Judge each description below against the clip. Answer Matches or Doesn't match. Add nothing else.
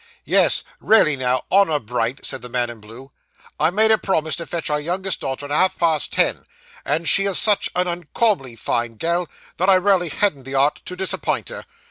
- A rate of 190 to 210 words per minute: Matches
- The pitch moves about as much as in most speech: Doesn't match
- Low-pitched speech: Doesn't match